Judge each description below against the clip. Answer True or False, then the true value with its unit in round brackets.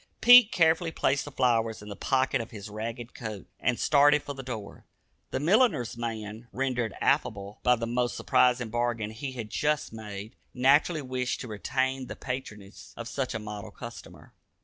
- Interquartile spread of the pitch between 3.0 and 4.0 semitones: True (3.5 semitones)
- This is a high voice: False (125 Hz)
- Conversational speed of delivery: True (170 wpm)